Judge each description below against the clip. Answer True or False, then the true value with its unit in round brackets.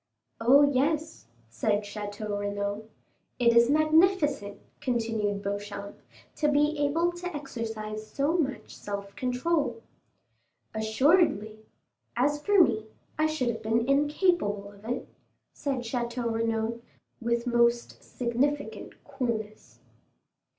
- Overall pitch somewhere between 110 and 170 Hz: False (235 Hz)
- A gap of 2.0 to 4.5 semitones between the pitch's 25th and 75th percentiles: False (5.1 semitones)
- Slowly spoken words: True (110 wpm)